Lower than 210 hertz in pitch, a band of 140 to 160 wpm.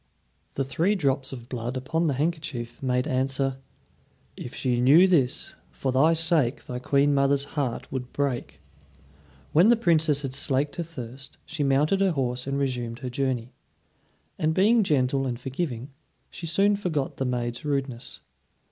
Yes: low, 135 Hz; average, 155 wpm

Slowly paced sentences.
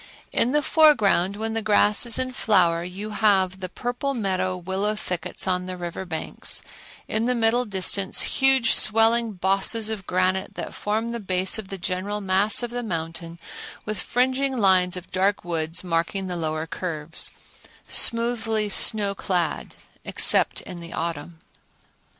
No: average, 155 wpm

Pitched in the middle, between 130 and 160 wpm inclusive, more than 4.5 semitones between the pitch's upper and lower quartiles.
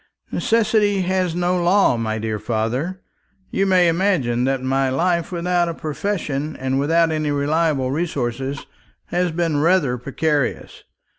Yes: medium, 160 Hz; slow, 135 wpm; average, 5.0 semitones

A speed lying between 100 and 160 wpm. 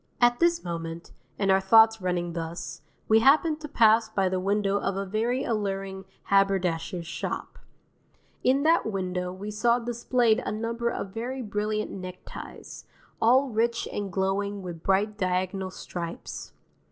Yes: average, 145 wpm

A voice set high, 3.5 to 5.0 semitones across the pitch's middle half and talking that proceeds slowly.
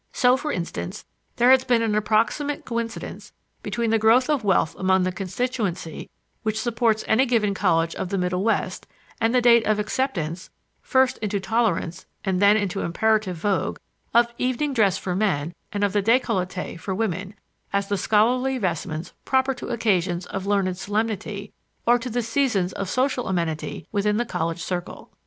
No: high, 210 Hz; average, 4.1 semitones; average, 170 wpm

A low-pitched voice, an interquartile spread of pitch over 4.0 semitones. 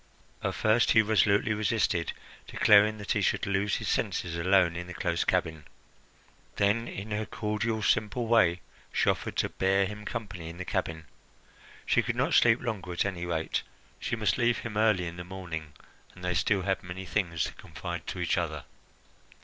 No: very low, 95 Hz; average, 3.5 semitones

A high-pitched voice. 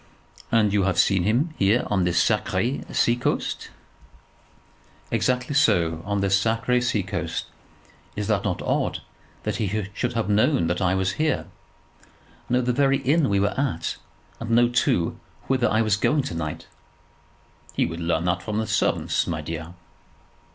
No: low, 105 Hz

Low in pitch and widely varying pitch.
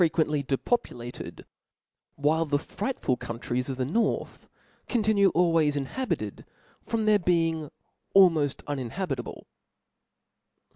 No: medium, 160 Hz; wide, 6.1 semitones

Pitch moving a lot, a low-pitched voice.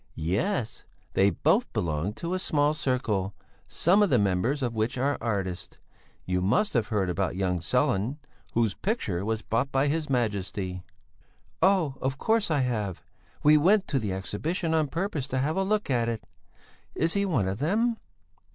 Yes: wide, 8.2 semitones; low, 125 Hz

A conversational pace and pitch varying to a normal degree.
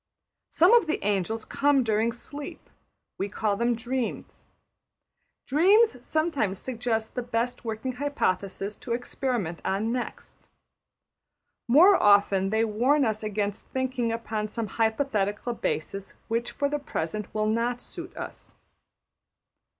No: slow, 125 wpm; average, 3.6 semitones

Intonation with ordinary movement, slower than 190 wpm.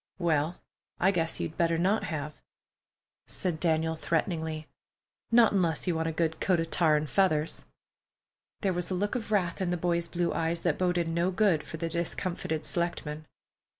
No: narrow, 2.0 semitones; average, 170 wpm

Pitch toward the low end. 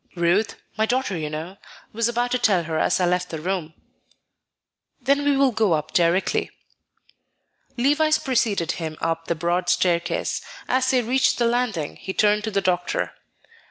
No: high, 195 Hz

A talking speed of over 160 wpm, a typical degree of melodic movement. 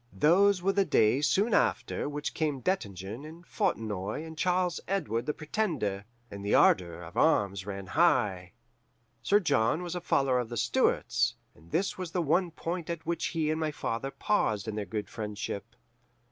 No: average, 175 wpm; wide, 8.8 semitones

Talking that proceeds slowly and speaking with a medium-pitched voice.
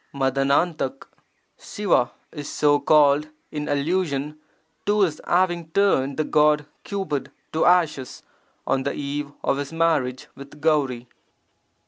Yes: slow, 125 wpm; medium, 150 Hz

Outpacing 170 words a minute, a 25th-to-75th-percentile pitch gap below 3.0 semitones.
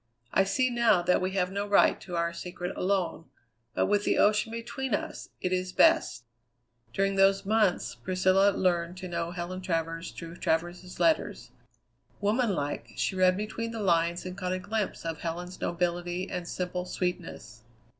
No: average, 165 wpm; narrow, 2.5 semitones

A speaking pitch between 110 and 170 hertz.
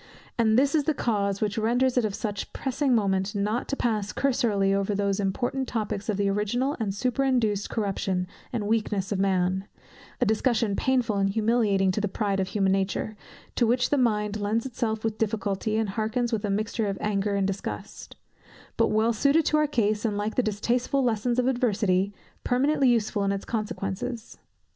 No: high, 215 Hz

